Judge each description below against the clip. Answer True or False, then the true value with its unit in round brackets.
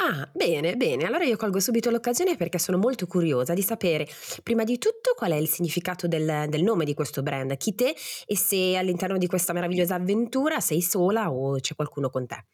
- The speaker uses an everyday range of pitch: False (5.9 semitones)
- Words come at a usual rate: False (205 wpm)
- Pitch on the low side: False (180 Hz)